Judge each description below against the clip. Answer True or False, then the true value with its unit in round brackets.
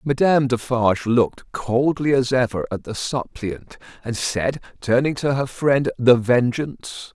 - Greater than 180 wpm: False (145 wpm)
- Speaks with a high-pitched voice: False (125 Hz)